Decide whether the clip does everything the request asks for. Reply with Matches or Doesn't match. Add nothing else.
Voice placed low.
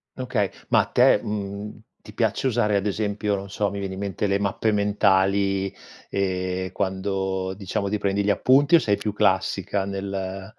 Matches